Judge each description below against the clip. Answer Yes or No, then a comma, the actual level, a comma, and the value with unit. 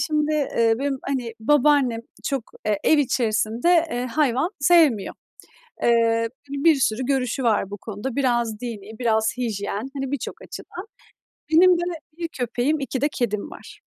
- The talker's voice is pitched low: No, very high, 250 Hz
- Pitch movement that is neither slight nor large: Yes, average, 4.0 semitones